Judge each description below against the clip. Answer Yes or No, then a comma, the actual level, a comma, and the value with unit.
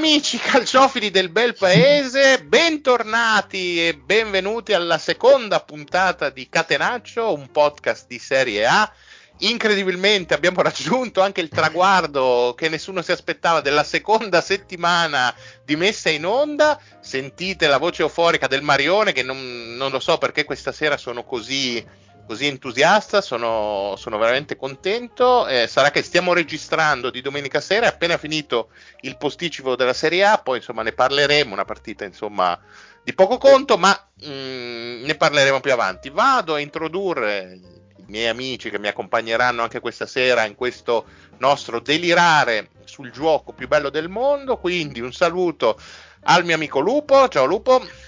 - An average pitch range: No, wide, 7.6 semitones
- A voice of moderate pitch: Yes, medium, 160 Hz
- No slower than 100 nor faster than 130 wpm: No, average, 150 wpm